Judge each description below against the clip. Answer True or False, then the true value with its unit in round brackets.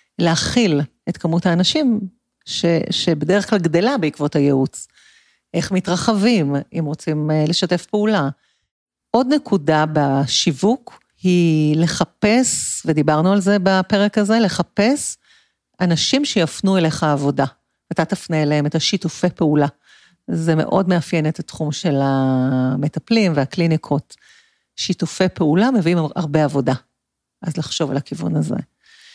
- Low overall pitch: False (170 Hz)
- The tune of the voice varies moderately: True (4.8 semitones)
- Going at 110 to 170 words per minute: True (115 wpm)